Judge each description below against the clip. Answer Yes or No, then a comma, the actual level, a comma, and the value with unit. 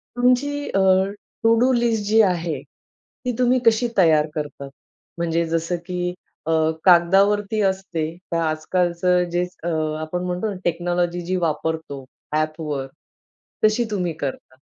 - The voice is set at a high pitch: No, medium, 175 Hz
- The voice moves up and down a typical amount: Yes, average, 4.1 semitones